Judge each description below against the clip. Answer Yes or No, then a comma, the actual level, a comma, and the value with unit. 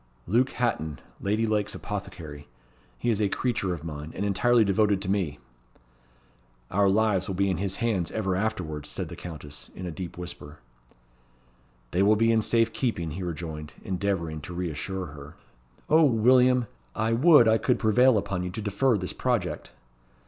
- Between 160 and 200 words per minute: Yes, average, 170 wpm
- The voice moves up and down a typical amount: Yes, average, 4.4 semitones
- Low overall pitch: Yes, low, 100 Hz